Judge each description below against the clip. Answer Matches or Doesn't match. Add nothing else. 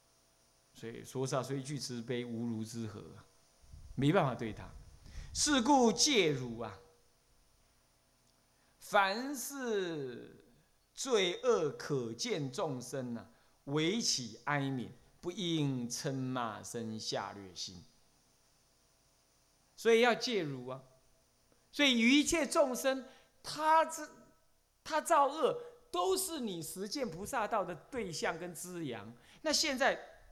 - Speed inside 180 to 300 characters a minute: Doesn't match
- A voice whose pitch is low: Matches